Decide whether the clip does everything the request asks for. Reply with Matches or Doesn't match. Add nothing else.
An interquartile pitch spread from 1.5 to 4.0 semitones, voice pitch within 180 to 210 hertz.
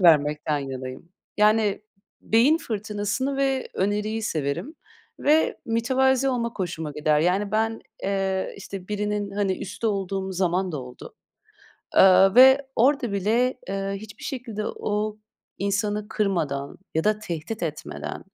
Matches